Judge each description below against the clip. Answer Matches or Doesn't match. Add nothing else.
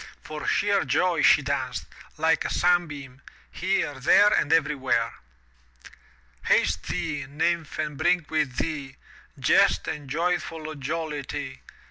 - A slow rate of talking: Matches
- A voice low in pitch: Doesn't match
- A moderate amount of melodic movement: Matches